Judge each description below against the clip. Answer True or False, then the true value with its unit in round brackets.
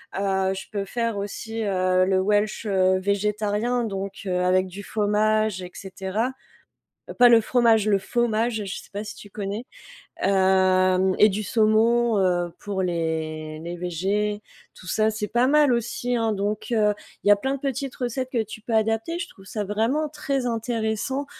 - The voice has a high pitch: True (210 Hz)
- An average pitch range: True (3.2 semitones)